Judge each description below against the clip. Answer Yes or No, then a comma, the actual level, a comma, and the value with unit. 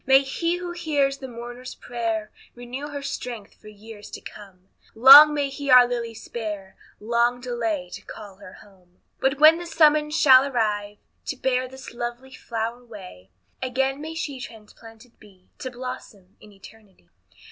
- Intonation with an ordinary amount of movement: Yes, average, 4.2 semitones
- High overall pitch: Yes, high, 240 Hz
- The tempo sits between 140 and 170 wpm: Yes, average, 160 wpm